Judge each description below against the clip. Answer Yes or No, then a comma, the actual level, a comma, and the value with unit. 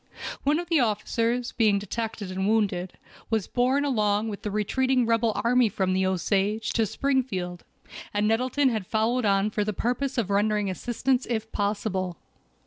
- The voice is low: No, high, 220 Hz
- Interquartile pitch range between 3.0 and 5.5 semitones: Yes, average, 3.4 semitones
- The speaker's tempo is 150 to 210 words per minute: Yes, average, 160 wpm